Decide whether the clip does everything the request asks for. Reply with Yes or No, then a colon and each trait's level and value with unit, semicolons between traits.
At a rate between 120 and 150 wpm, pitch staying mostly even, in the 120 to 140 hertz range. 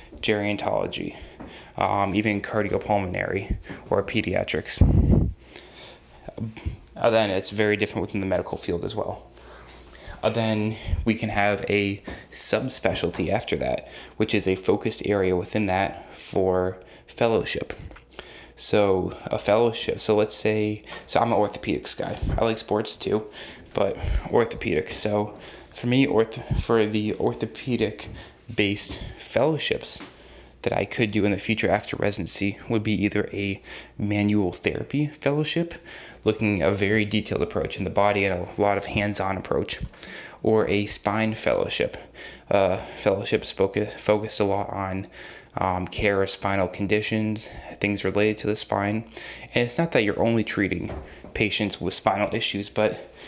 No: average, 140 wpm; narrow, 1.9 semitones; low, 105 Hz